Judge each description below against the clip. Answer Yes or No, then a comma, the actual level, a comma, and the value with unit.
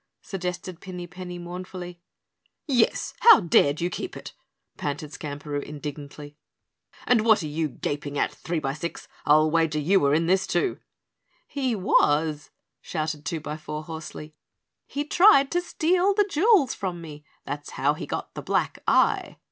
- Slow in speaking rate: No, average, 145 wpm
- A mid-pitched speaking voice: Yes, medium, 170 Hz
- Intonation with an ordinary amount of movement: Yes, average, 4.7 semitones